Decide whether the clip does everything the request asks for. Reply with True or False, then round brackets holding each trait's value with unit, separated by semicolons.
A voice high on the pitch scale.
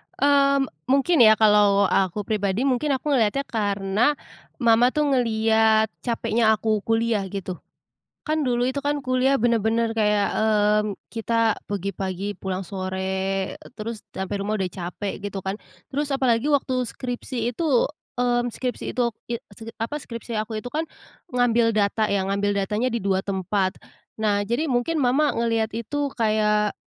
True (225 Hz)